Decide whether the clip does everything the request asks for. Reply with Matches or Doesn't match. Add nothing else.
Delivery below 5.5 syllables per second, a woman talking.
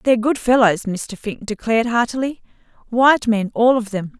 Matches